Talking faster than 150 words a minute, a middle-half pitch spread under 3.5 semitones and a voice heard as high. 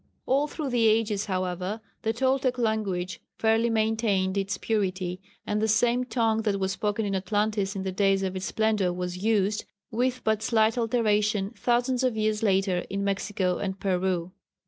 Yes: average, 170 wpm; average, 2.8 semitones; high, 210 Hz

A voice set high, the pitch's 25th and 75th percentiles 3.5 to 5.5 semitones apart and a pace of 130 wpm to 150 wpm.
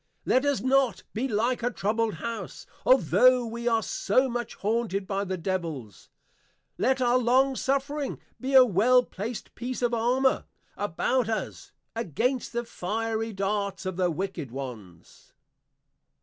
Yes: high, 230 Hz; average, 4.6 semitones; average, 140 wpm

